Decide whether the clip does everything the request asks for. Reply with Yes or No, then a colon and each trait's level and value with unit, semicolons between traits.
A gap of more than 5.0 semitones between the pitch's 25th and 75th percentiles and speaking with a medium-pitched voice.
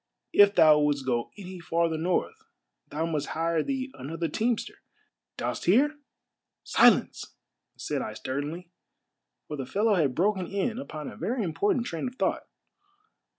Yes: wide, 5.5 semitones; medium, 170 Hz